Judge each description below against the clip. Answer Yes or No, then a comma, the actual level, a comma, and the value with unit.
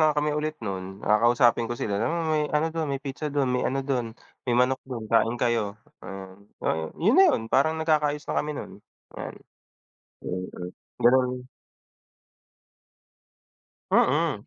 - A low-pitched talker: Yes, low, 130 Hz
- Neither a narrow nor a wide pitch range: Yes, average, 4.8 semitones